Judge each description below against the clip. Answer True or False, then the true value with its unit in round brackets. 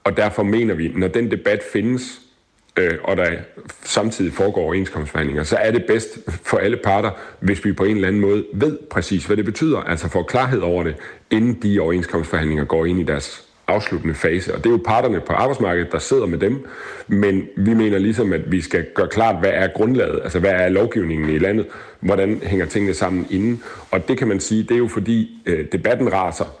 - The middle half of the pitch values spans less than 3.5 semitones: False (4.1 semitones)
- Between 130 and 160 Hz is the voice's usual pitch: False (100 Hz)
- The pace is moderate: True (210 wpm)